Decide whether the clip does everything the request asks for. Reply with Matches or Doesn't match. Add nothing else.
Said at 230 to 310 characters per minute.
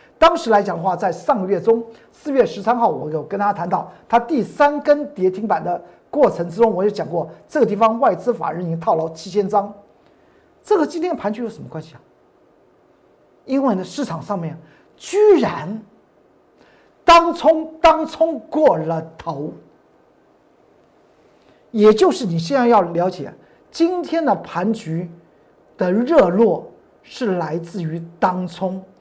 Doesn't match